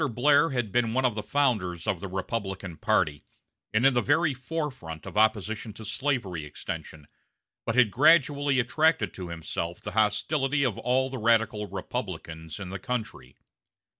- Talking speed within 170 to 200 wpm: No, average, 160 wpm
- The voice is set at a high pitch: No, low, 110 Hz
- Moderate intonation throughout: No, wide, 5.7 semitones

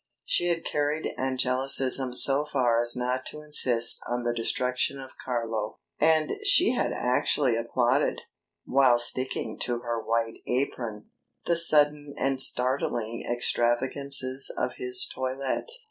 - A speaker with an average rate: No, slow, 130 wpm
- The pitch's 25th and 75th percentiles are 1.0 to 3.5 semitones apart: Yes, average, 3.0 semitones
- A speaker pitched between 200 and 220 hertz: No, low, 130 Hz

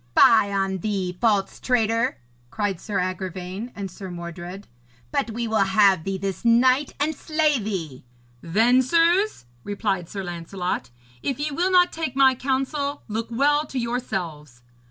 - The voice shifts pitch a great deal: Yes, wide, 5.7 semitones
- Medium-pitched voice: No, high, 215 Hz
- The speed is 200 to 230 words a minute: No, average, 150 wpm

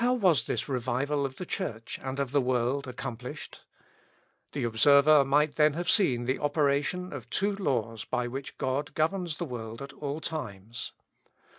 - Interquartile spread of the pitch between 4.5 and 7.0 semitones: No, average, 3.8 semitones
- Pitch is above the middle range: No, medium, 140 Hz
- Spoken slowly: No, average, 165 wpm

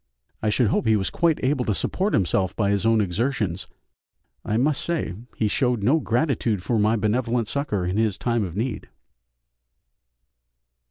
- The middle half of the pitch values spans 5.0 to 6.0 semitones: No, average, 3.8 semitones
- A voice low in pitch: Yes, low, 110 Hz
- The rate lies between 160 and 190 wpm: Yes, average, 165 wpm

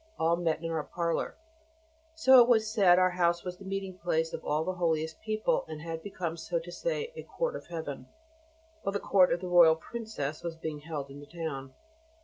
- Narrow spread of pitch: No, average, 3.5 semitones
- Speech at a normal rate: No, fast, 215 wpm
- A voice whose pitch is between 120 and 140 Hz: No, medium, 170 Hz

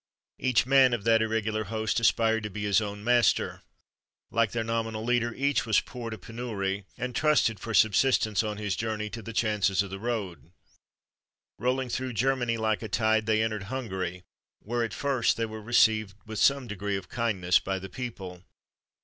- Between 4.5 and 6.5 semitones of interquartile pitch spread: No, narrow, 2.5 semitones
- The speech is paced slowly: No, average, 180 wpm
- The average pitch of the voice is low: Yes, low, 110 Hz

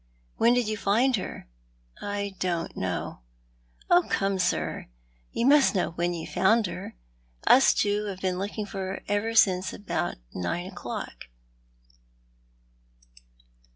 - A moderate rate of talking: No, slow, 130 wpm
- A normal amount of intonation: Yes, average, 3.2 semitones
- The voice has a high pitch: Yes, high, 200 Hz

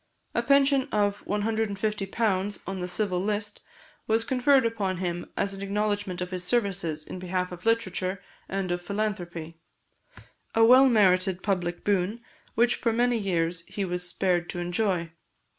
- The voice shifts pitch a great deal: No, average, 3.5 semitones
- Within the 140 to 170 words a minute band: Yes, average, 150 wpm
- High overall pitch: Yes, high, 195 Hz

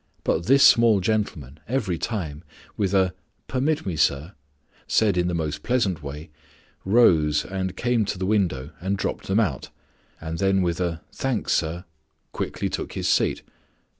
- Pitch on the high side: No, very low, 95 Hz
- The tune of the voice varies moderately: Yes, average, 5.0 semitones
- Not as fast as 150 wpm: No, average, 160 wpm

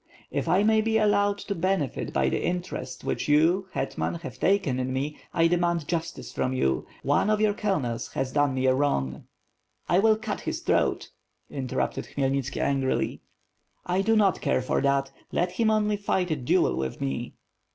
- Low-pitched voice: No, medium, 165 Hz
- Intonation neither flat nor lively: No, wide, 7.1 semitones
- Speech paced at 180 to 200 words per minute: Yes, average, 185 wpm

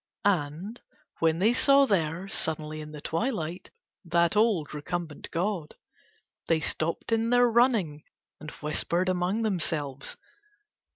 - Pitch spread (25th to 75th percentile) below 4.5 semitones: No, wide, 5.5 semitones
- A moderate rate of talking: No, slow, 120 wpm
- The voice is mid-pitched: Yes, medium, 170 Hz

